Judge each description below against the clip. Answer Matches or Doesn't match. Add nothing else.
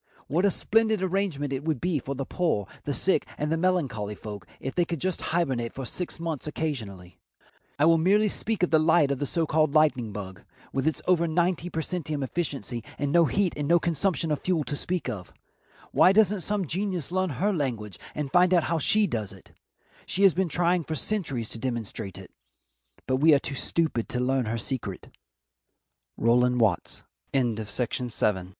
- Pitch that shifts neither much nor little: Doesn't match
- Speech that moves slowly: Doesn't match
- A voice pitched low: Doesn't match